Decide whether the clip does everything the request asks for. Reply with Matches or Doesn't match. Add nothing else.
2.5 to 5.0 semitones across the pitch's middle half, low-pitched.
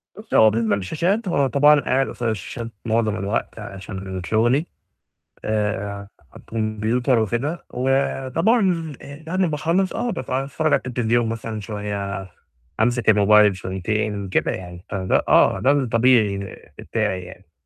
Doesn't match